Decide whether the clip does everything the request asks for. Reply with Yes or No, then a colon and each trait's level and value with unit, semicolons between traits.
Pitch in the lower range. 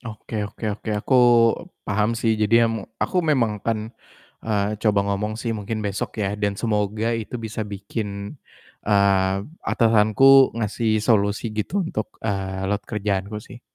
Yes: low, 105 Hz